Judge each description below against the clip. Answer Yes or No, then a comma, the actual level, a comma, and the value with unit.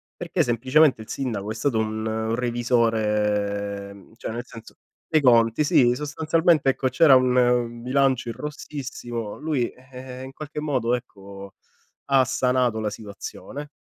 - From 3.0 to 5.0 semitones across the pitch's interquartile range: Yes, average, 3.3 semitones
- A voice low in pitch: Yes, low, 120 Hz